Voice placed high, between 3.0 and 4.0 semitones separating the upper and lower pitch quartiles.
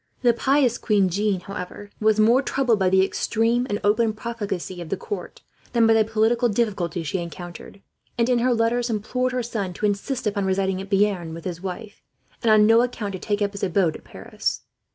Yes: high, 210 Hz; average, 3.5 semitones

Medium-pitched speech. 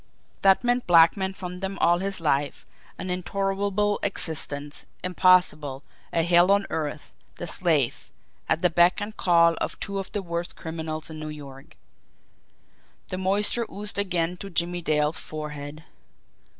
Yes: medium, 175 Hz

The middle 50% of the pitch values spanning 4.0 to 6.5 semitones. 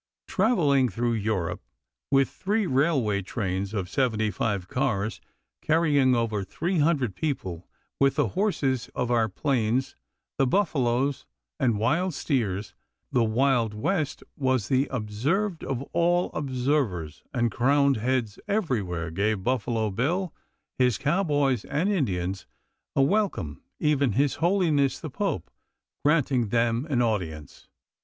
Yes: wide, 5.5 semitones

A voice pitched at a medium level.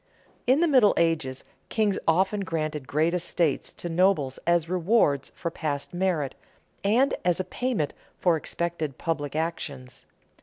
Yes: medium, 170 Hz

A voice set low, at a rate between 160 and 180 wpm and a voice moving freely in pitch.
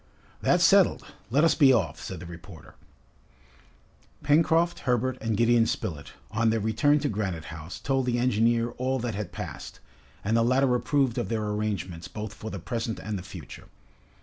No: low, 115 Hz; average, 175 wpm; average, 4.0 semitones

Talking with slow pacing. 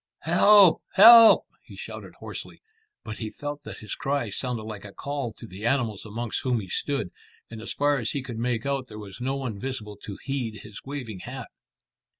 No: average, 195 wpm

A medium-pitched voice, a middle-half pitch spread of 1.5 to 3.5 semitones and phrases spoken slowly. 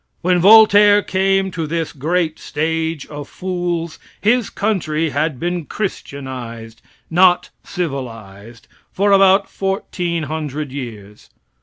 No: medium, 165 Hz; average, 5.2 semitones; slow, 110 wpm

